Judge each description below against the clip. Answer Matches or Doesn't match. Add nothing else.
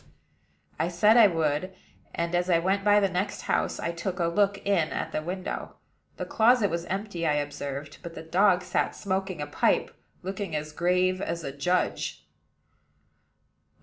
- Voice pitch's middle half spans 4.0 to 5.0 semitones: Doesn't match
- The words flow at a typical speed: Matches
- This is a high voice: Doesn't match